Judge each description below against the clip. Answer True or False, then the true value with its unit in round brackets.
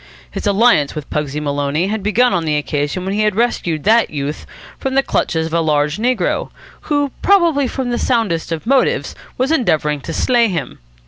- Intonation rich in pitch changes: True (8.3 semitones)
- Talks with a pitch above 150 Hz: True (190 Hz)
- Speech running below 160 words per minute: False (190 wpm)